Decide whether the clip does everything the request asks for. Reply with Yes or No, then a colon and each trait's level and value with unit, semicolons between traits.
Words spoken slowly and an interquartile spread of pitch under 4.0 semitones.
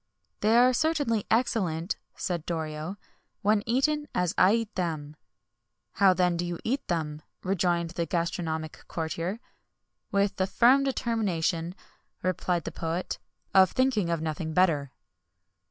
No: slow, 130 wpm; average, 4.9 semitones